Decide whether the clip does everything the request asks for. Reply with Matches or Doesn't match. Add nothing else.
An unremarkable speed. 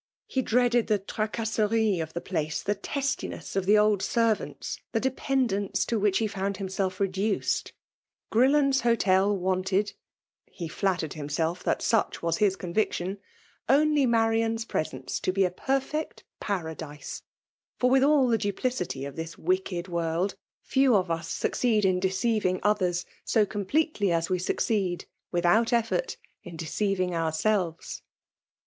Doesn't match